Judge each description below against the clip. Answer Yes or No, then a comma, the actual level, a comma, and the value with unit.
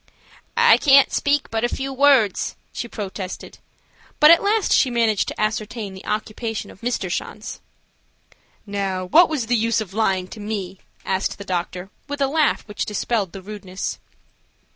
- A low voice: No, high, 215 Hz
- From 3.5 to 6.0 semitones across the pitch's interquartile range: Yes, average, 5.2 semitones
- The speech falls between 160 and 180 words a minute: Yes, average, 165 wpm